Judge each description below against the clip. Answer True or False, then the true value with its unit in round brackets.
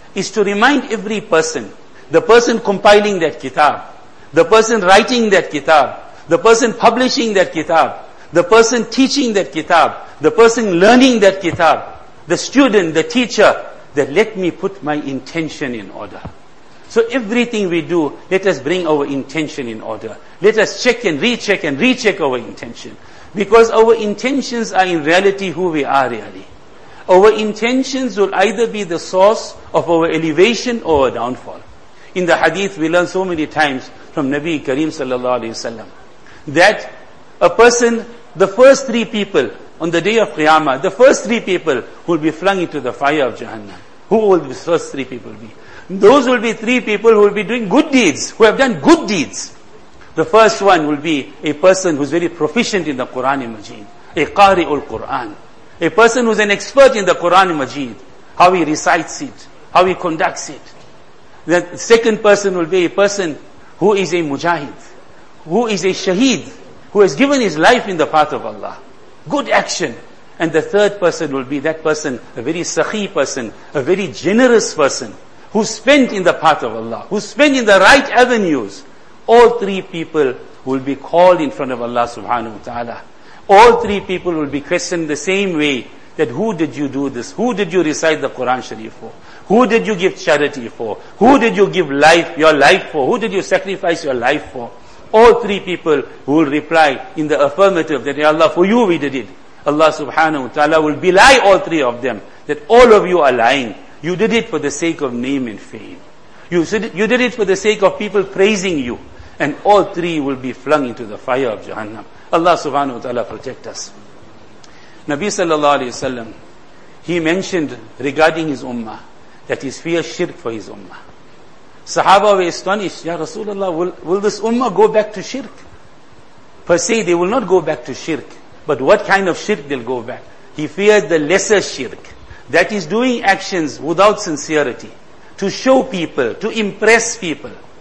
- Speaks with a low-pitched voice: False (180 Hz)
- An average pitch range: False (5.9 semitones)